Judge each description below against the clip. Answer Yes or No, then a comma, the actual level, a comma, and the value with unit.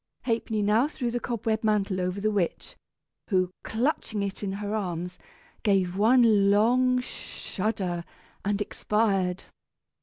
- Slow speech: Yes, slow, 125 wpm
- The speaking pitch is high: Yes, high, 210 Hz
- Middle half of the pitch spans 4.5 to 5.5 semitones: No, average, 2.9 semitones